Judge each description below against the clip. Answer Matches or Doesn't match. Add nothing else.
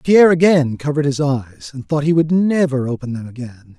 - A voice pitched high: Doesn't match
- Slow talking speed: Doesn't match